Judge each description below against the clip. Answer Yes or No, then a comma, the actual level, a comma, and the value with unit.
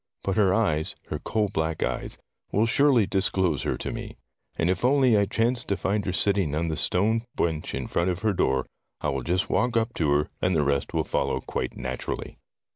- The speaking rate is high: Yes, fast, 210 wpm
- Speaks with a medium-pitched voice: No, very low, 95 Hz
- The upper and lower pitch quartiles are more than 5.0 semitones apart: Yes, wide, 5.6 semitones